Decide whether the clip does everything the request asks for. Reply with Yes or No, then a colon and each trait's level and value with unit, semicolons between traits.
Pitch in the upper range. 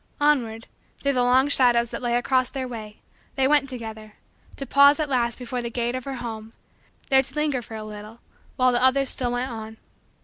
Yes: high, 245 Hz